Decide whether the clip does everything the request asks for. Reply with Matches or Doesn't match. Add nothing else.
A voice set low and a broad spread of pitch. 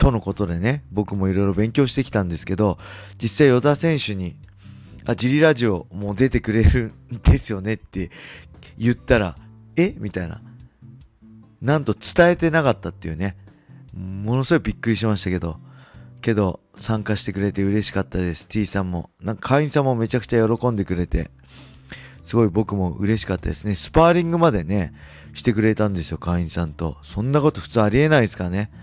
Doesn't match